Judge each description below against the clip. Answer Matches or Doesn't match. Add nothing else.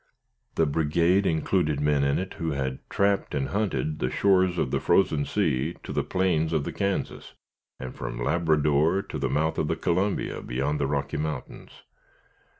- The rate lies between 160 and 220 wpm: Matches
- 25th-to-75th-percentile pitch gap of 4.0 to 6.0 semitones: Matches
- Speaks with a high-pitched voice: Doesn't match